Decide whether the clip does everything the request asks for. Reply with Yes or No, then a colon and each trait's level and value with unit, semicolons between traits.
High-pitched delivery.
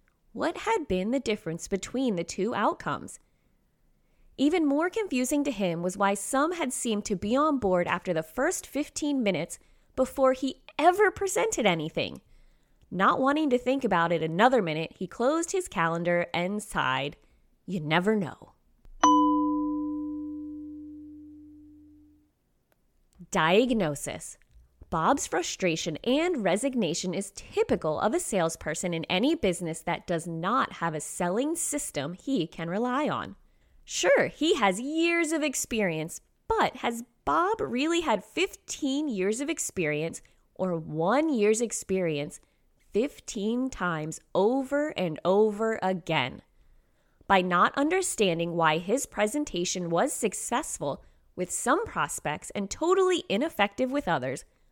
Yes: high, 225 Hz